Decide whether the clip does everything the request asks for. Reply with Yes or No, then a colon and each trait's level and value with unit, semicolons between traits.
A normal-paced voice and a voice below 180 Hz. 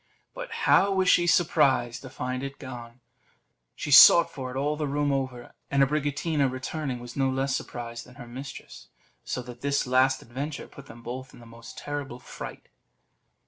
Yes: average, 180 wpm; low, 135 Hz